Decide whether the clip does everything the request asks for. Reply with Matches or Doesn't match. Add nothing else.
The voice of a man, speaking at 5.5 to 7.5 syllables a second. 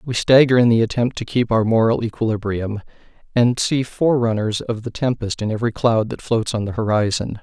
Matches